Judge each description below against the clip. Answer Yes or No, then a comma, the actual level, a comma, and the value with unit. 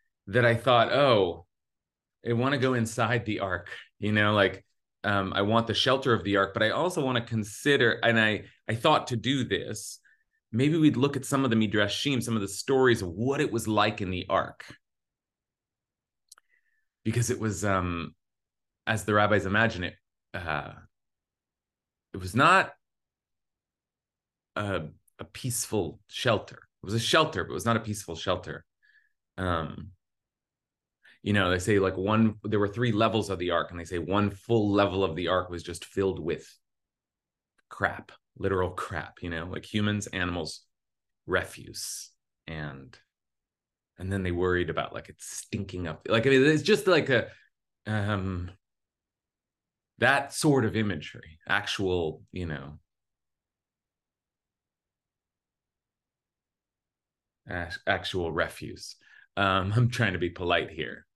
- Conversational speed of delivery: Yes, average, 150 wpm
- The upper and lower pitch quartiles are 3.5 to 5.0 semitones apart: Yes, average, 4.2 semitones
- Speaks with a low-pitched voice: Yes, low, 105 Hz